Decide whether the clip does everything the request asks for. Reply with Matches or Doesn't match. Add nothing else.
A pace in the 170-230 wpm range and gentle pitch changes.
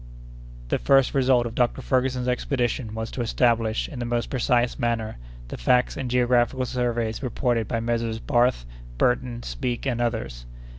Doesn't match